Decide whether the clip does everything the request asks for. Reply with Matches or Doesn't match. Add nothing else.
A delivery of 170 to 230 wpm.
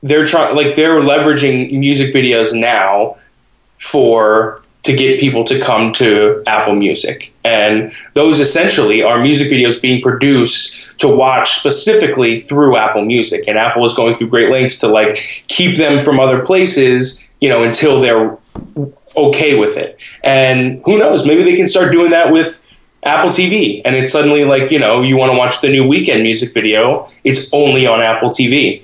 Matches